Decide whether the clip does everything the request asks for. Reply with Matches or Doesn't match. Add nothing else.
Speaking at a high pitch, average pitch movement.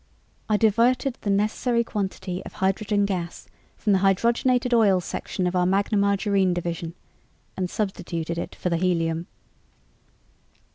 Matches